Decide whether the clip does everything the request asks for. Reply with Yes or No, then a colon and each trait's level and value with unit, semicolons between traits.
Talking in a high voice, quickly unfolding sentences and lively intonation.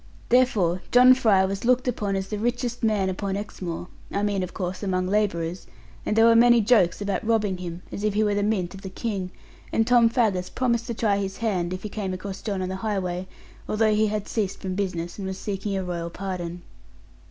No: high, 200 Hz; fast, 220 wpm; average, 3.0 semitones